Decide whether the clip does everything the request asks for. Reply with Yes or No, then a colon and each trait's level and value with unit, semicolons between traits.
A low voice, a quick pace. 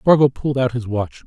Yes: low, 125 Hz; fast, 235 wpm